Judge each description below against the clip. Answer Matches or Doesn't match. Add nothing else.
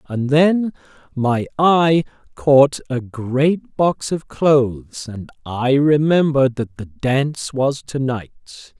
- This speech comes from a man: Matches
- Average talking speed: Doesn't match